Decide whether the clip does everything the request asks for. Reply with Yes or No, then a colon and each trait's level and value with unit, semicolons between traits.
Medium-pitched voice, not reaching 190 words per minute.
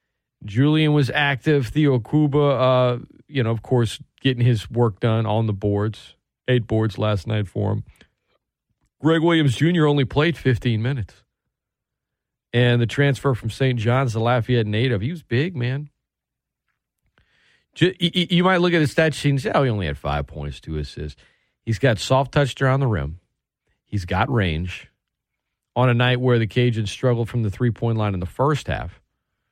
No: low, 125 Hz; average, 175 wpm